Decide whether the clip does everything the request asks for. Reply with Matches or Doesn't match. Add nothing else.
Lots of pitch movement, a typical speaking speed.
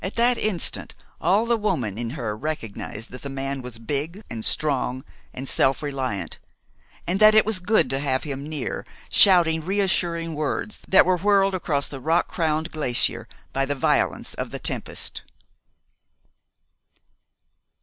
Matches